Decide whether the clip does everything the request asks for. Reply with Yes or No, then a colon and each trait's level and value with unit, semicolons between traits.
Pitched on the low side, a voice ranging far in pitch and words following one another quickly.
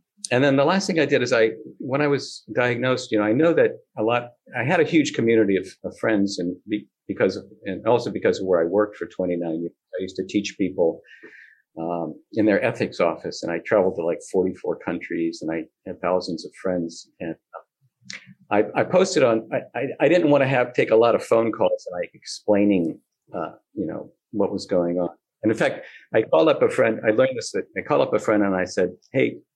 Yes: low, 110 Hz; wide, 8.7 semitones; fast, 230 wpm